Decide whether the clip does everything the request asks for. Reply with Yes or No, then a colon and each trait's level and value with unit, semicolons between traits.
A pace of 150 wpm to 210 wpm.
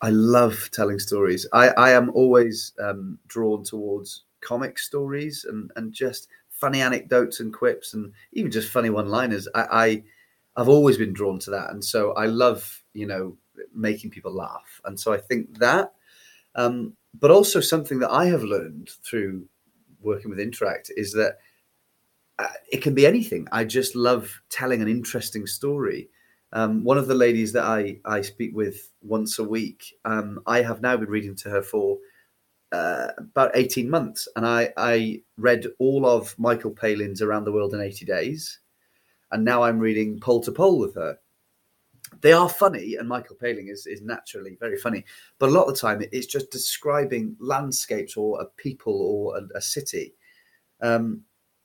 Yes: average, 175 wpm